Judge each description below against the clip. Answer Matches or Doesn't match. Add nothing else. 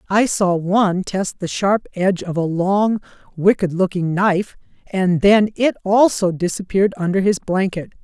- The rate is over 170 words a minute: Doesn't match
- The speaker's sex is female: Matches